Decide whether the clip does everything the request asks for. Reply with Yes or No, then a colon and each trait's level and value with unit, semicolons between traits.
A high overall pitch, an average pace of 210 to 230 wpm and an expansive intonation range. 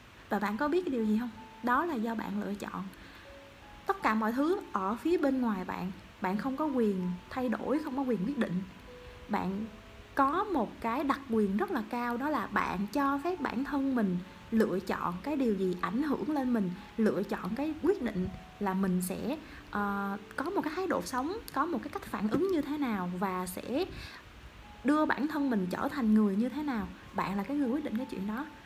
Yes: high, 235 Hz; average, 220 wpm; wide, 6.0 semitones